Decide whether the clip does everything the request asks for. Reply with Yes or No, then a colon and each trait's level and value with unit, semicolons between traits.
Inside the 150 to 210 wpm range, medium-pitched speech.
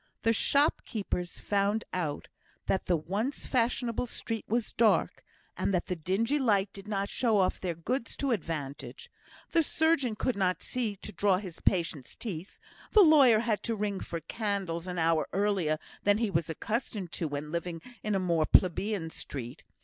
No: average, 170 wpm; high, 200 Hz